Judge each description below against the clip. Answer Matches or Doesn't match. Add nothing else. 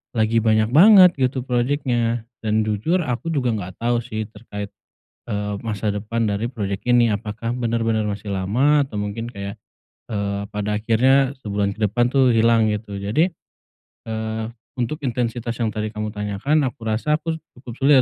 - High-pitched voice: Doesn't match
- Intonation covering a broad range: Doesn't match